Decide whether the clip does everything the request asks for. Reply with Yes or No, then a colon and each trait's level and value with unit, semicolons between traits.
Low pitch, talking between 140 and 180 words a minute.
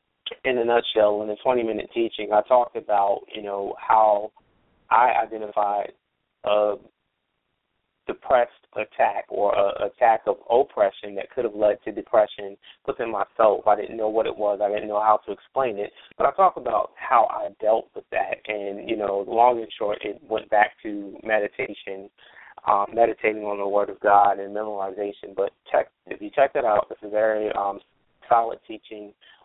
Yes: low, 105 Hz; average, 175 wpm